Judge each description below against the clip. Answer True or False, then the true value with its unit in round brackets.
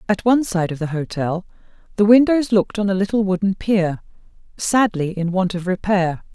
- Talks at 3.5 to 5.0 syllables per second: False (5.4 syllables/s)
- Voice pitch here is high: True (195 Hz)